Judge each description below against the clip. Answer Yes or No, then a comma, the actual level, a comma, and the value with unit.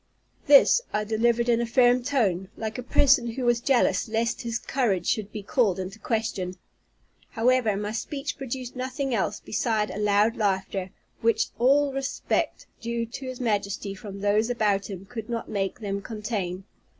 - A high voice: Yes, high, 225 Hz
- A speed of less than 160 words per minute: No, average, 170 wpm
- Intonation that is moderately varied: Yes, average, 3.3 semitones